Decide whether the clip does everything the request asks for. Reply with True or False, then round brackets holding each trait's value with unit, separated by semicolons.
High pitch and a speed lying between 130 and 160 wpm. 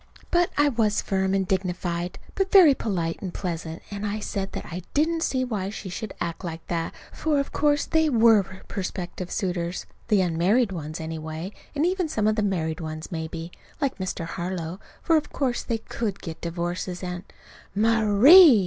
False (195 Hz; 175 wpm)